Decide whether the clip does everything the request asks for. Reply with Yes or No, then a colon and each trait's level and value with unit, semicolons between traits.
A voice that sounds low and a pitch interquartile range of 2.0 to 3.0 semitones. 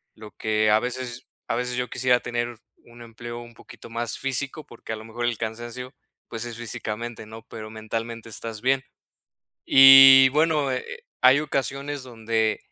Yes: low, 120 Hz; narrow, 2.5 semitones